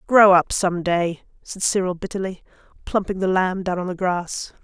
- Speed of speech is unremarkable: Yes, average, 180 wpm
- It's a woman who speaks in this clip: Yes, female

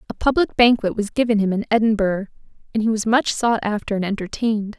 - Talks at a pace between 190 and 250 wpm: Yes, average, 200 wpm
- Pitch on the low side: No, high, 215 Hz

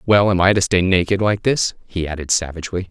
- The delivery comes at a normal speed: No, fast, 225 wpm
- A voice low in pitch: Yes, very low, 95 Hz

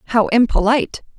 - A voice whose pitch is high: Yes, high, 245 Hz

